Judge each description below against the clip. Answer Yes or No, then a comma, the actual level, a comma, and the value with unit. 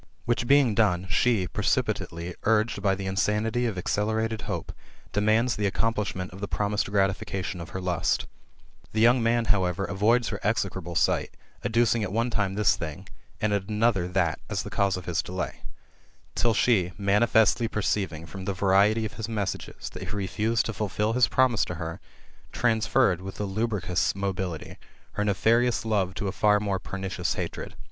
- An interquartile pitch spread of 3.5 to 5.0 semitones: No, average, 2.9 semitones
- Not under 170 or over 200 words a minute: Yes, average, 175 wpm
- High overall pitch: No, low, 105 Hz